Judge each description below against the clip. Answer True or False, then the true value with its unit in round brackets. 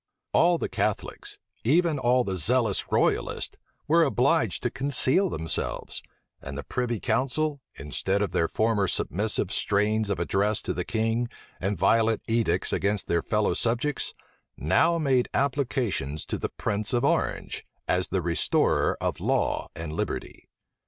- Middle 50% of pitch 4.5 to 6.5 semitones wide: True (5.2 semitones)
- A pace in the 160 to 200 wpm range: False (145 wpm)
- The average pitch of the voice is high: False (115 Hz)